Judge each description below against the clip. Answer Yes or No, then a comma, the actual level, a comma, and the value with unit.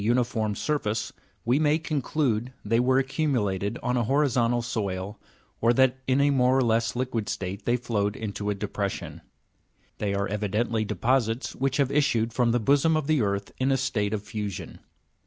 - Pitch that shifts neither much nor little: Yes, average, 4.0 semitones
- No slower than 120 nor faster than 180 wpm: Yes, average, 175 wpm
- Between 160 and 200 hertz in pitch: No, low, 120 Hz